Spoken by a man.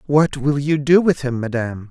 Yes: male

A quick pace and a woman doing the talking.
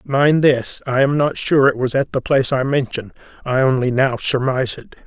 No: fast, 215 wpm; male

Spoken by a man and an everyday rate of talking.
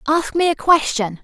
No: female; average, 195 wpm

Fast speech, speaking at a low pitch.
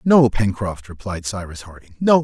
No: average, 160 wpm; low, 110 Hz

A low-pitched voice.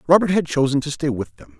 No: medium, 145 Hz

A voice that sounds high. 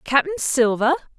Yes: very high, 285 Hz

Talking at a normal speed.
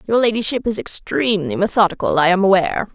Yes: average, 165 wpm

